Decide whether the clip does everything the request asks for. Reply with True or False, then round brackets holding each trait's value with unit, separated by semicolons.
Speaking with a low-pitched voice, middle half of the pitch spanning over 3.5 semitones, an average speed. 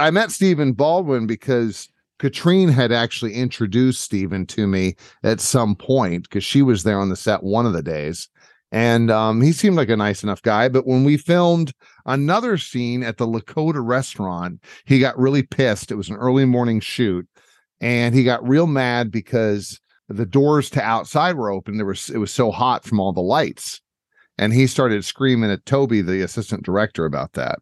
True (120 Hz; 4.3 semitones; 190 wpm)